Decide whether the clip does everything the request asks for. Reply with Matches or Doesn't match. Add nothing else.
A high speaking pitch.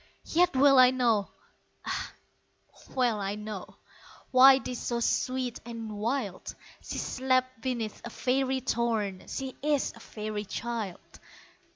Matches